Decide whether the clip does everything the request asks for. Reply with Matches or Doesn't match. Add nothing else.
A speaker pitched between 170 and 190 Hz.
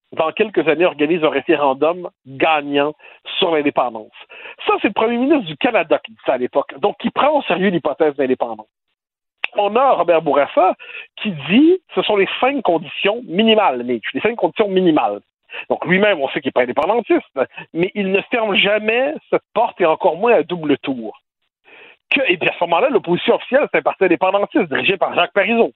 Matches